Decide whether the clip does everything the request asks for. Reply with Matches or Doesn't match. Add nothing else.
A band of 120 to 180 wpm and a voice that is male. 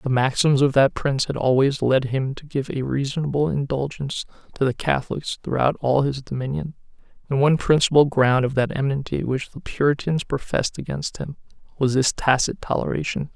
Matches